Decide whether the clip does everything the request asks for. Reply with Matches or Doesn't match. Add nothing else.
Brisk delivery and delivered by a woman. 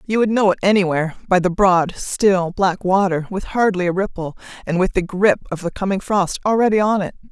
Matches